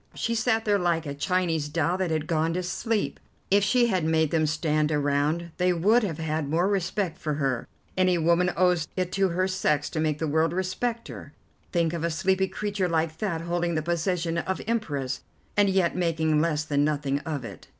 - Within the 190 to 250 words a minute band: Yes, average, 200 wpm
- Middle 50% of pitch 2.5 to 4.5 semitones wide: Yes, average, 3.1 semitones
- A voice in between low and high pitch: Yes, medium, 170 Hz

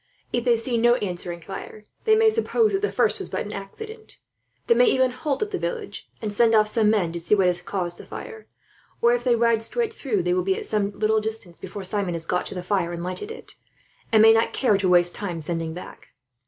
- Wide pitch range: Yes, wide, 6.0 semitones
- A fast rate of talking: Yes, fast, 245 wpm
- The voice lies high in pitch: Yes, high, 215 Hz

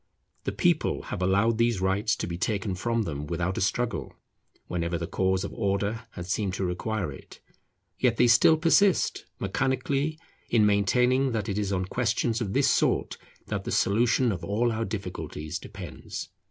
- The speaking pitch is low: Yes, low, 105 Hz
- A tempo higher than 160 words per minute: Yes, average, 170 wpm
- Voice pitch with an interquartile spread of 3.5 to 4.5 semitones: Yes, average, 4.1 semitones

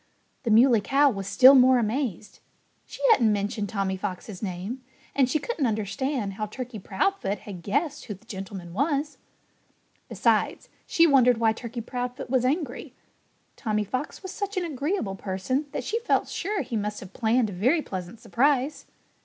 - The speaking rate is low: No, average, 165 wpm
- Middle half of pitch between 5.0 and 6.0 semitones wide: Yes, wide, 5.4 semitones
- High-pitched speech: Yes, high, 240 Hz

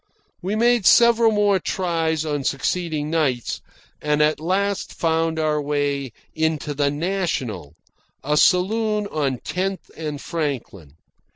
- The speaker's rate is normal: No, slow, 120 wpm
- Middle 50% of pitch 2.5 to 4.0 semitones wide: No, average, 4.6 semitones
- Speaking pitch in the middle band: Yes, medium, 160 Hz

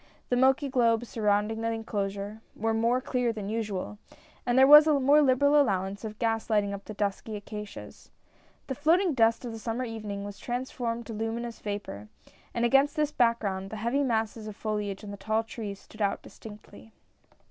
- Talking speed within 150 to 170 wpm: No, average, 185 wpm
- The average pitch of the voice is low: No, high, 225 Hz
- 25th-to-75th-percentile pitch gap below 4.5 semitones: Yes, average, 3.0 semitones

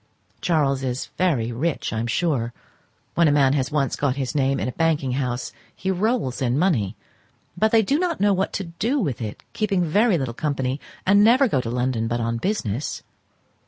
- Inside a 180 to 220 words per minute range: Yes, average, 195 wpm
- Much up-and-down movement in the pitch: Yes, wide, 7.2 semitones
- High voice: No, medium, 145 Hz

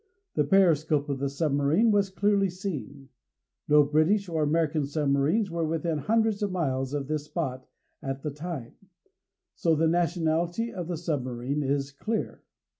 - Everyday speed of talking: Yes, average, 150 wpm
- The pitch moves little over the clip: No, average, 4.0 semitones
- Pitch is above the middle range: No, medium, 155 Hz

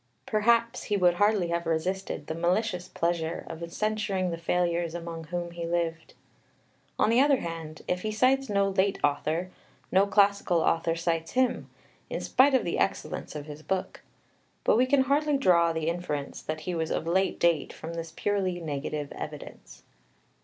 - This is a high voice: No, medium, 175 Hz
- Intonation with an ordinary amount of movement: Yes, average, 3.7 semitones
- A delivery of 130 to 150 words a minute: No, average, 170 wpm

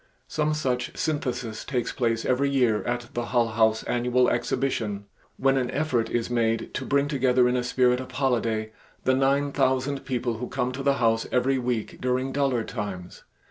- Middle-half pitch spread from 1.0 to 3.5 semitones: Yes, narrow, 2.5 semitones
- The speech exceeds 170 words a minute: Yes, average, 180 wpm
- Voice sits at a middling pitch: No, low, 125 Hz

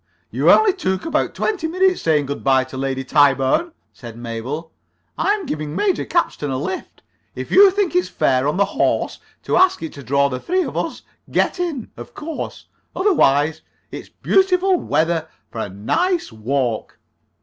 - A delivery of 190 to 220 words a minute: No, average, 170 wpm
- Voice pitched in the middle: Yes, medium, 160 Hz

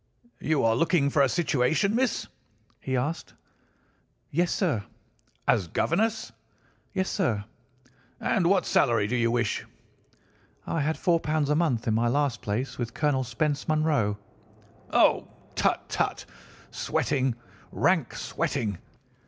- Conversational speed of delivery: No, slow, 125 wpm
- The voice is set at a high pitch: No, medium, 140 Hz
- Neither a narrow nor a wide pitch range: No, wide, 5.9 semitones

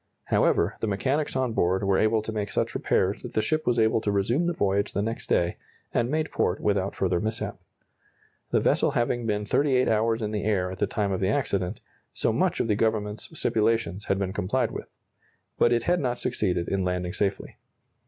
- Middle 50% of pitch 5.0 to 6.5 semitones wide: No, average, 3.3 semitones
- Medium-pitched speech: No, low, 105 Hz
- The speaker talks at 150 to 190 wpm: No, fast, 205 wpm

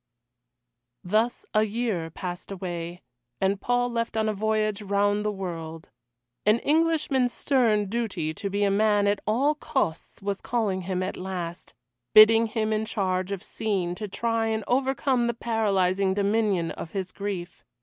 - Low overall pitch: No, high, 205 Hz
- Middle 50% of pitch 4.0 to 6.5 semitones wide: No, average, 3.2 semitones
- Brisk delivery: No, average, 155 wpm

